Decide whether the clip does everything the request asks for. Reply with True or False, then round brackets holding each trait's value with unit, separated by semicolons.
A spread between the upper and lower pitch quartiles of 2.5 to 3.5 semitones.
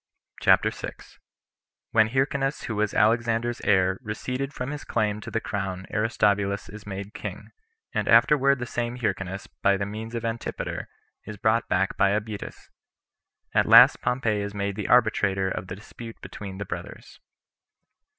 True (2.9 semitones)